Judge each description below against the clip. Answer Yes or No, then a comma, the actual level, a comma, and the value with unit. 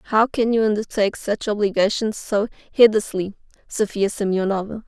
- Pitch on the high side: Yes, high, 210 Hz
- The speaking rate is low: Yes, slow, 125 wpm